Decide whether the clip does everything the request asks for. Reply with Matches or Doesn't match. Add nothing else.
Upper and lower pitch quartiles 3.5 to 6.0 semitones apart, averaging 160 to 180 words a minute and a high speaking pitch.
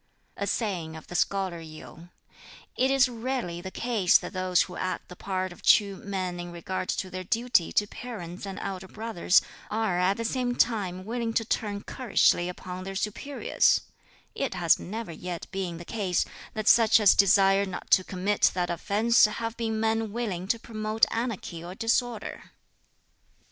Matches